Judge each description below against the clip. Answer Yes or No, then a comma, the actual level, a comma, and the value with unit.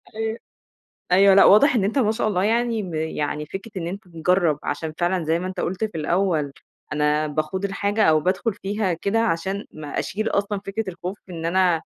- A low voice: No, high, 190 Hz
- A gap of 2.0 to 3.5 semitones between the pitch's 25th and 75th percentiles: No, average, 4.1 semitones